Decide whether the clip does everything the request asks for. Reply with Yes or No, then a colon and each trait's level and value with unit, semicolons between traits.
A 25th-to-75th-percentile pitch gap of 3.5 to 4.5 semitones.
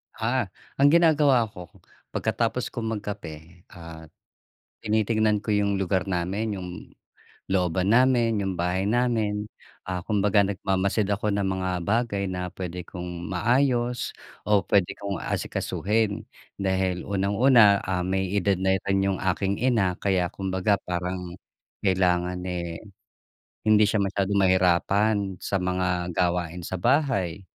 No: average, 2.8 semitones